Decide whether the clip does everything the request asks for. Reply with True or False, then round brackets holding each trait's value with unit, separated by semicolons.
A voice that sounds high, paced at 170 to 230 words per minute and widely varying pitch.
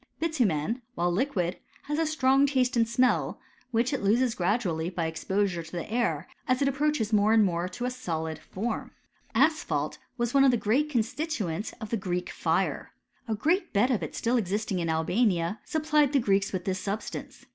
True (220 Hz; 185 wpm; 6.2 semitones)